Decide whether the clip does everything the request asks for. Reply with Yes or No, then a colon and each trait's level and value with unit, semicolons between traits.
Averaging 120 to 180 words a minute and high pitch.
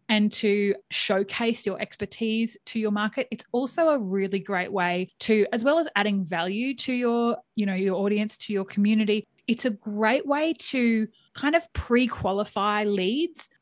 Yes: average, 165 wpm; high, 215 Hz